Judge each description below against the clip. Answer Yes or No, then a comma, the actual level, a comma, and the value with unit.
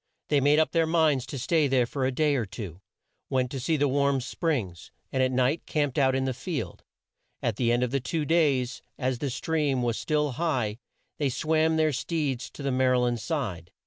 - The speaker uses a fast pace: Yes, fast, 210 wpm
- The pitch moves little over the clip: No, average, 3.4 semitones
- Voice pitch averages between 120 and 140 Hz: Yes, low, 135 Hz